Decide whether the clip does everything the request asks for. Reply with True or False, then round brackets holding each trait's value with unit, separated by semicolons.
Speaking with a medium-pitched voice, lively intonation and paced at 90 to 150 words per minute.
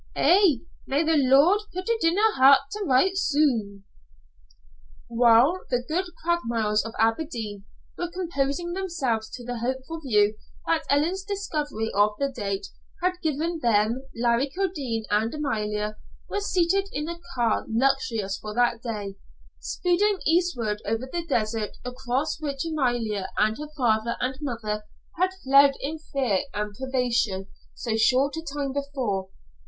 False (265 Hz; 6.4 semitones; 145 wpm)